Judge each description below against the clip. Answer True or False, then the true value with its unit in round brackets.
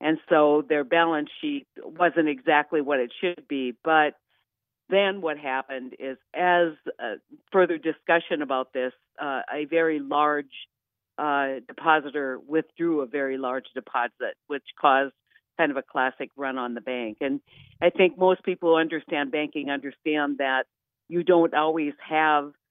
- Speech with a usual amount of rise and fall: True (3.6 semitones)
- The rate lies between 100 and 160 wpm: True (150 wpm)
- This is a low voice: False (150 Hz)